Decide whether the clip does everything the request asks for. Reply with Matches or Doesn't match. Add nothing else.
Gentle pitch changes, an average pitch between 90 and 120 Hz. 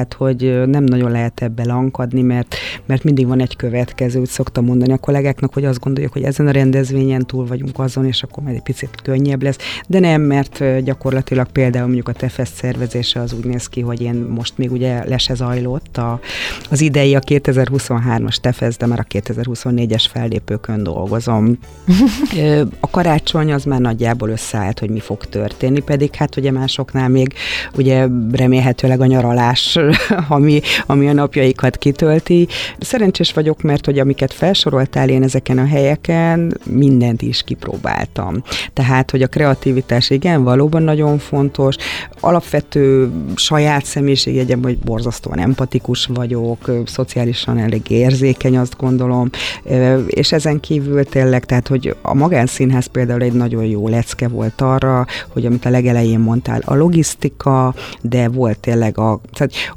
Doesn't match